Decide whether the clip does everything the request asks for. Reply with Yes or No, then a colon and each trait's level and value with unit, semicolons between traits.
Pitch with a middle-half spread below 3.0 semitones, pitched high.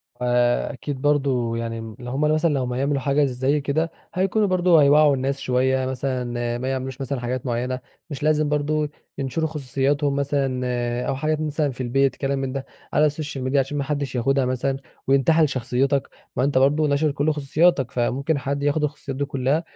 No: narrow, 2.4 semitones; medium, 140 Hz